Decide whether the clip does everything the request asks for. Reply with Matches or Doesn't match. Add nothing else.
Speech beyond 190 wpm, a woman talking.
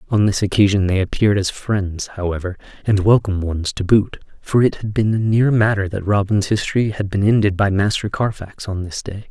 Doesn't match